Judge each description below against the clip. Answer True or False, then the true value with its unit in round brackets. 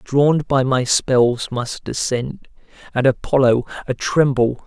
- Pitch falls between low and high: False (130 Hz)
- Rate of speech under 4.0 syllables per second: True (3.7 syllables/s)